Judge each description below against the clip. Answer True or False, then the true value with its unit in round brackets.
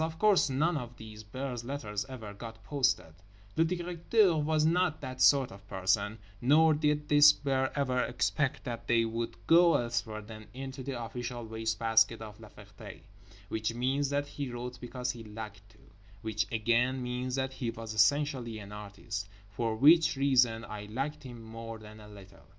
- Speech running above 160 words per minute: True (170 wpm)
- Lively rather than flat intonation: False (4.3 semitones)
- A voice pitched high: False (120 Hz)